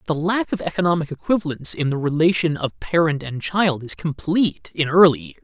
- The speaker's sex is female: No, male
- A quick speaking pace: No, average, 190 wpm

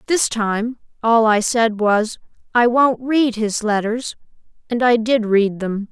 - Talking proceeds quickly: No, average, 160 wpm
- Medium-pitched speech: No, high, 225 Hz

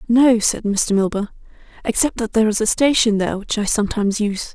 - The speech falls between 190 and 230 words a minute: Yes, average, 200 wpm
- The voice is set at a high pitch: Yes, high, 215 Hz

